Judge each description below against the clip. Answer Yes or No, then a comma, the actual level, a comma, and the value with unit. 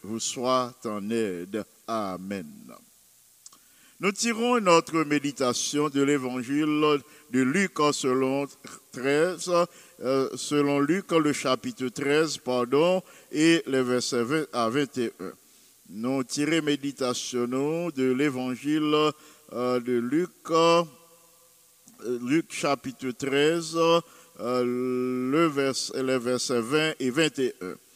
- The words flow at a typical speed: No, slow, 105 wpm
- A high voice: No, medium, 140 Hz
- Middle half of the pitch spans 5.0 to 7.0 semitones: No, average, 4.5 semitones